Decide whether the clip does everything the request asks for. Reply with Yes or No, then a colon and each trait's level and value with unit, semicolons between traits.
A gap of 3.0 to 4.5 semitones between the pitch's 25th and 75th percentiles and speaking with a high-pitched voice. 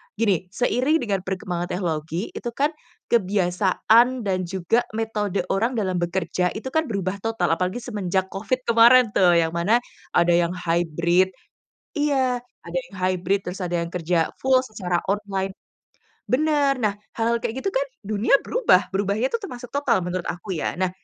No: average, 5.1 semitones; high, 200 Hz